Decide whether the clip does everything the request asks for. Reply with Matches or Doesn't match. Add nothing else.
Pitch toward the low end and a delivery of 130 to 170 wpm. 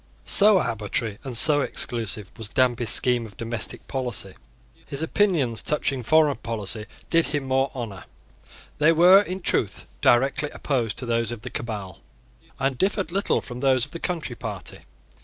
Matches